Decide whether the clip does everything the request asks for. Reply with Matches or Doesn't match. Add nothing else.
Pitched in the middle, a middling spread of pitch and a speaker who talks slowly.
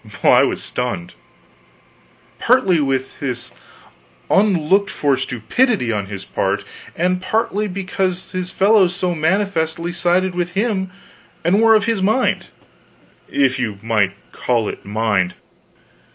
Doesn't match